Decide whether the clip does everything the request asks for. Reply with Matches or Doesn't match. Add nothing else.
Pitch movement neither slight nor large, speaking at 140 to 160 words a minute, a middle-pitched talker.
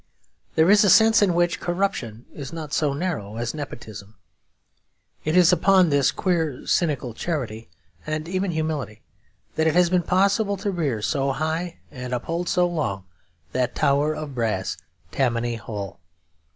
Doesn't match